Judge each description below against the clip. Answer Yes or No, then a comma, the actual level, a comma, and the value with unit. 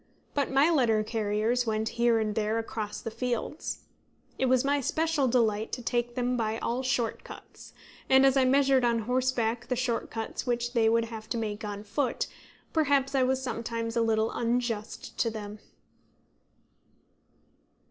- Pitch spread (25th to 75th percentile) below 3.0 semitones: Yes, narrow, 2.6 semitones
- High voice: Yes, high, 235 Hz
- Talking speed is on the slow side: No, average, 165 wpm